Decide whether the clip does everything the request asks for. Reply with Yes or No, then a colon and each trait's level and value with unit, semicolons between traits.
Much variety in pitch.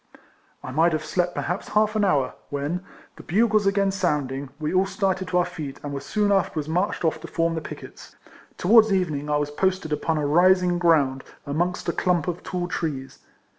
No: average, 4.0 semitones